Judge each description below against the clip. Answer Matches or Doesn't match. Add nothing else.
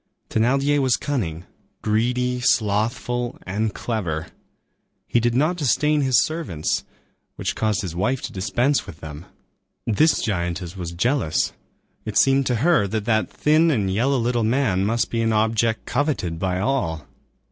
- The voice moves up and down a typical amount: Doesn't match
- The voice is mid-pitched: Doesn't match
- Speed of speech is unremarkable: Matches